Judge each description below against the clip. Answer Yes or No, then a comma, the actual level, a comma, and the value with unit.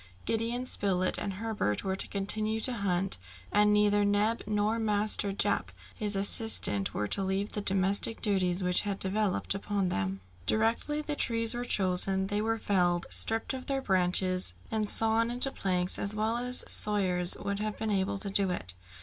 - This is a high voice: Yes, high, 205 Hz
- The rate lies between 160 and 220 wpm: Yes, average, 175 wpm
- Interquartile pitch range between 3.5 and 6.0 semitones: No, average, 2.7 semitones